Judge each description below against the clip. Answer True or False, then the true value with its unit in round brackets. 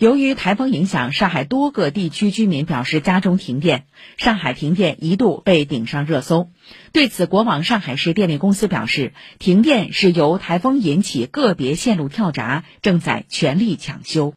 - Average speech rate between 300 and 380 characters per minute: False (265 characters per minute)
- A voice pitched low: False (185 Hz)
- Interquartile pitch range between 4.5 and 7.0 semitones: True (5.4 semitones)